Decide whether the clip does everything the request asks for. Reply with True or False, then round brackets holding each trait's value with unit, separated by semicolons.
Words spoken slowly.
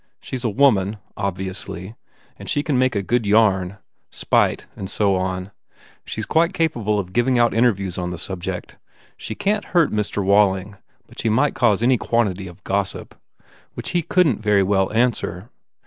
False (180 wpm)